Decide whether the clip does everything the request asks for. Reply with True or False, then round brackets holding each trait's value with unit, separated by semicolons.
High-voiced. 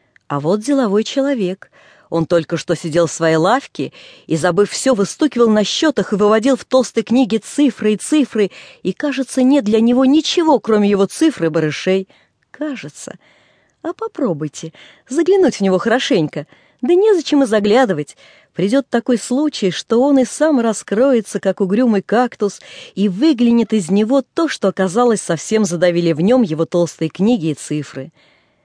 True (220 Hz)